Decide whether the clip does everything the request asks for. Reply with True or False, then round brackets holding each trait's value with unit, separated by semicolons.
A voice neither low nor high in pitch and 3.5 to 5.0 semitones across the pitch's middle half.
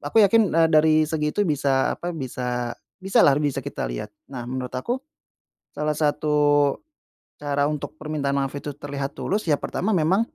False (150 Hz; 2.4 semitones)